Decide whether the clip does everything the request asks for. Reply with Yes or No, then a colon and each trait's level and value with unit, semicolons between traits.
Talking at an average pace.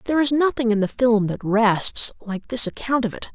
No: fast, 235 wpm